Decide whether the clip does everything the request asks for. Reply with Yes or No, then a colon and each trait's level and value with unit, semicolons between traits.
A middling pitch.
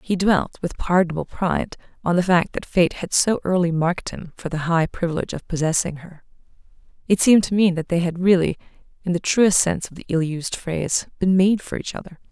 Yes: medium, 175 Hz